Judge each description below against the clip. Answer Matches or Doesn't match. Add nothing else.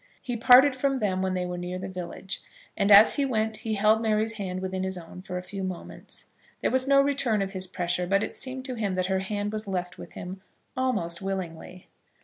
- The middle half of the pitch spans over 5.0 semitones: Doesn't match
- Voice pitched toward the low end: Doesn't match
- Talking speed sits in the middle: Doesn't match